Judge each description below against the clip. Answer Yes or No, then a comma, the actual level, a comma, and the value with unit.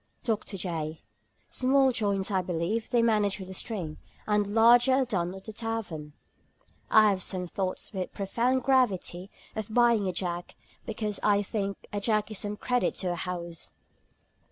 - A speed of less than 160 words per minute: No, average, 170 wpm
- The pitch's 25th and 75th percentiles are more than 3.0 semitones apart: Yes, average, 3.6 semitones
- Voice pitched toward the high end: Yes, high, 205 Hz